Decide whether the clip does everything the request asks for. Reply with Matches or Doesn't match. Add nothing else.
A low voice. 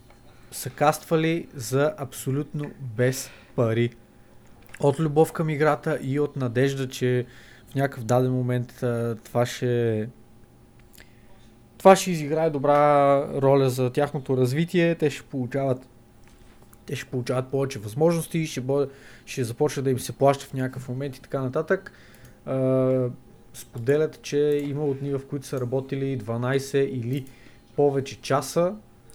Matches